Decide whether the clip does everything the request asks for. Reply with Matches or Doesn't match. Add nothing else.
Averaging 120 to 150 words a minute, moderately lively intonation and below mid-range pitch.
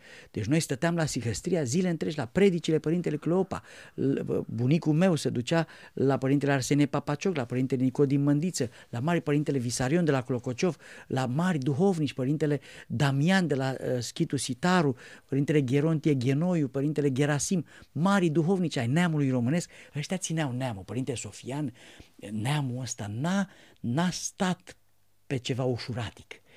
Doesn't match